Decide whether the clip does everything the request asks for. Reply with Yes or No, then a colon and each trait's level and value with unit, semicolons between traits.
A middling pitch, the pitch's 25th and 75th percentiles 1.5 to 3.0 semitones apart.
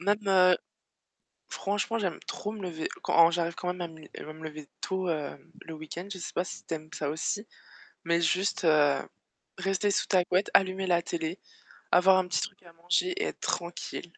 Yes: medium, 180 Hz; narrow, 2.5 semitones